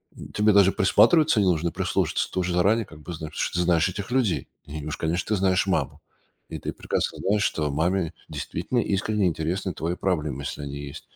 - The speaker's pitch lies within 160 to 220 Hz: No, very low, 90 Hz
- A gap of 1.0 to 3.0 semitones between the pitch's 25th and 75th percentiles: No, average, 4.2 semitones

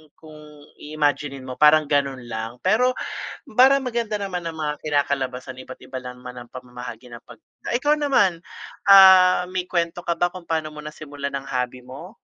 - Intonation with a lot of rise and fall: Yes, wide, 5.8 semitones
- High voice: No, medium, 150 Hz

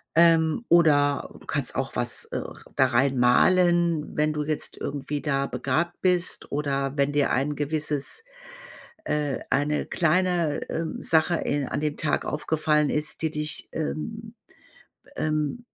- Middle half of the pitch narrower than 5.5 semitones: Yes, narrow, 2.6 semitones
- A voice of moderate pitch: Yes, medium, 150 Hz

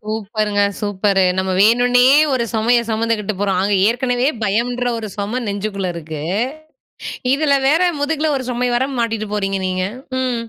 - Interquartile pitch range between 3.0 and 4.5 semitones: Yes, average, 3.5 semitones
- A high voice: Yes, high, 220 Hz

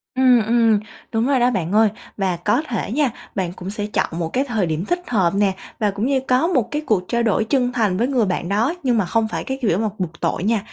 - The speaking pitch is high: Yes, high, 220 Hz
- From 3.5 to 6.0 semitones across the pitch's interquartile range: Yes, average, 4.2 semitones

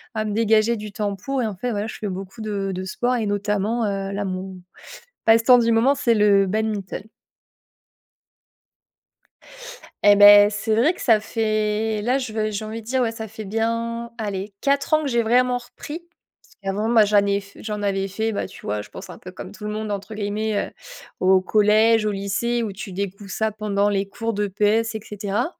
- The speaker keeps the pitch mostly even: Yes, narrow, 2.1 semitones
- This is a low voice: No, high, 215 Hz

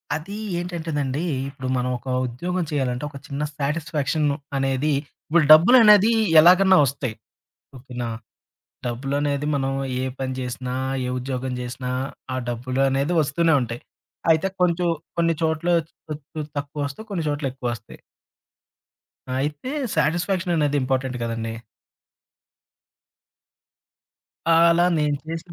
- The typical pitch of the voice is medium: Yes, medium, 145 Hz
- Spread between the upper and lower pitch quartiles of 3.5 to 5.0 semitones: Yes, average, 4.2 semitones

